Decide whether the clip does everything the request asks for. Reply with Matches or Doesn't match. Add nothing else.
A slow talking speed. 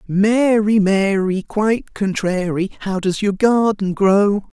Matches